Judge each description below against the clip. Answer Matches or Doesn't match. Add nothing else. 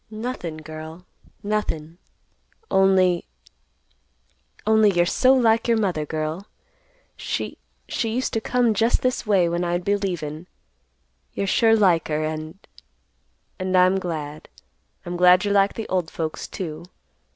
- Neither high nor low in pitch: Matches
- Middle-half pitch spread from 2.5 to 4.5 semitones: Doesn't match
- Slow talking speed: Matches